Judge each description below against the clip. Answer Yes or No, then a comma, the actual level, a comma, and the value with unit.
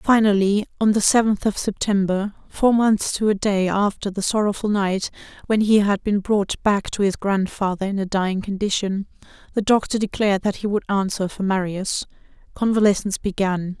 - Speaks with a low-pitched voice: No, high, 200 Hz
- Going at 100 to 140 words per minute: No, average, 170 wpm